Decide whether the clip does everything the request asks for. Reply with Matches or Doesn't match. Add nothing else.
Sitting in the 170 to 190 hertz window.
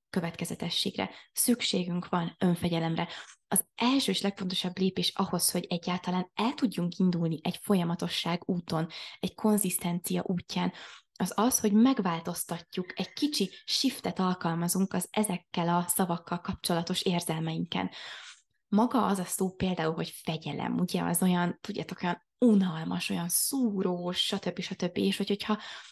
Matches